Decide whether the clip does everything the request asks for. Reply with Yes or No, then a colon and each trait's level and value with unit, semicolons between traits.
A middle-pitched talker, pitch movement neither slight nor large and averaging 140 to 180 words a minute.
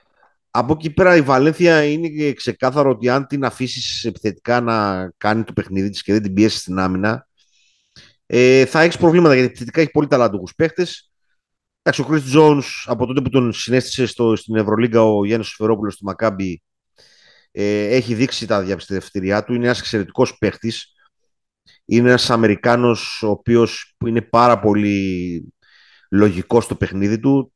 No: low, 120 Hz; average, 4.3 semitones; average, 150 wpm